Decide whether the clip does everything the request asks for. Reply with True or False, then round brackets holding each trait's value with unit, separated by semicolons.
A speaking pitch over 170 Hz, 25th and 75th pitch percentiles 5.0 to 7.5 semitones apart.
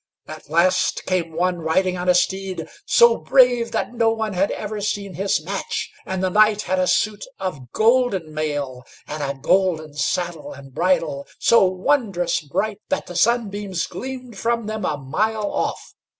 False (185 Hz; 4.6 semitones)